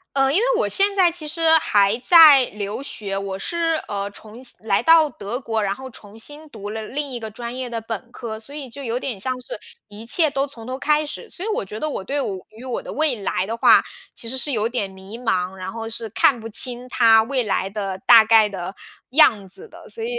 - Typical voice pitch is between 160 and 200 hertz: No, high, 235 Hz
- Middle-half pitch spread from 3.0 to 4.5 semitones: No, average, 5.1 semitones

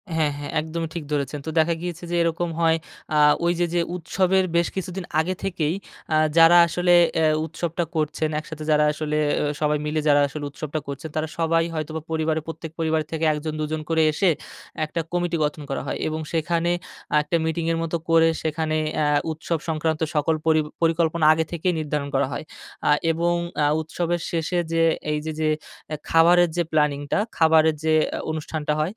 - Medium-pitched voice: Yes, medium, 160 Hz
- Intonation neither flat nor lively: No, narrow, 1.6 semitones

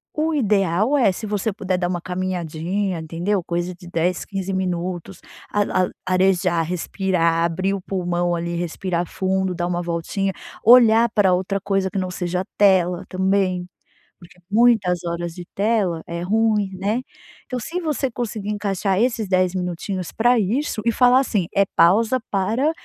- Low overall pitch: No, high, 190 Hz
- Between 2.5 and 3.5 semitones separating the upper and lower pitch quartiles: Yes, average, 3.0 semitones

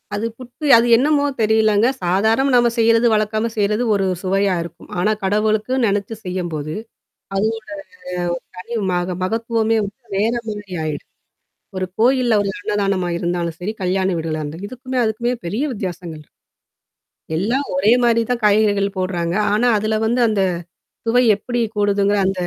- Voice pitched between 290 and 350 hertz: No, high, 210 Hz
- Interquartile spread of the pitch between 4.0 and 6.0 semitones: No, average, 3.5 semitones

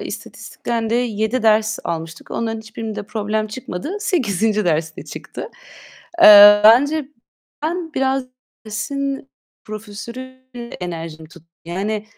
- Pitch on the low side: No, high, 220 Hz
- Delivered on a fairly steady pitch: No, average, 4.1 semitones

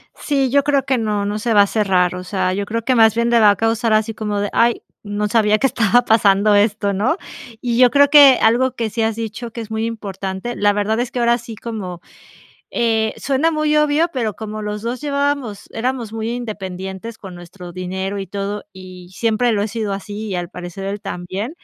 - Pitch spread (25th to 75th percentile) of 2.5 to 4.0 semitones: Yes, average, 3.0 semitones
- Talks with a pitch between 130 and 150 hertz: No, high, 220 Hz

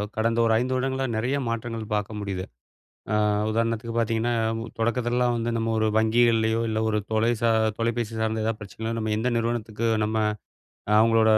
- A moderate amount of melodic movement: No, narrow, 1.1 semitones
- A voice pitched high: No, low, 115 Hz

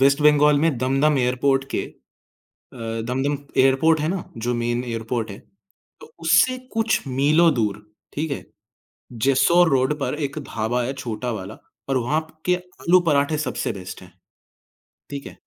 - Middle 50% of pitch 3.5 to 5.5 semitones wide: Yes, average, 4.1 semitones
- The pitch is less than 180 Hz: Yes, low, 135 Hz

